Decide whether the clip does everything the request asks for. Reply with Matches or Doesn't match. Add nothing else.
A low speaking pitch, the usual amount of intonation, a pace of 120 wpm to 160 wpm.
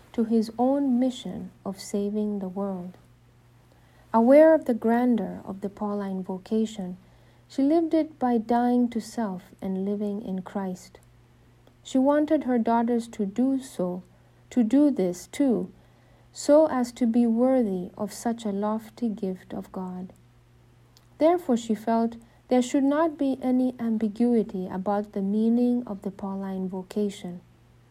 Doesn't match